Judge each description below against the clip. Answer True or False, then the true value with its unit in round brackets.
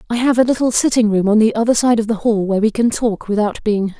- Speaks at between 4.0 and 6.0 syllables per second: False (6.6 syllables/s)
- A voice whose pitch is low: False (220 Hz)